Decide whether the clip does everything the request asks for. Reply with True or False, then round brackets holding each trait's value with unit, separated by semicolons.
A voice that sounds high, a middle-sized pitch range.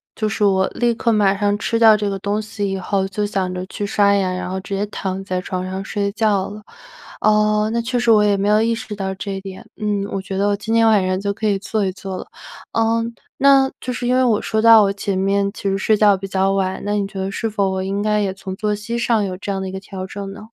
False (200 Hz; 1.9 semitones)